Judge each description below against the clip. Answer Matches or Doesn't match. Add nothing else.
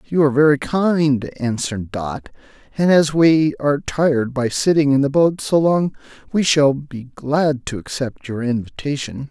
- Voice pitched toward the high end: Doesn't match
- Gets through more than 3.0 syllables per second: Matches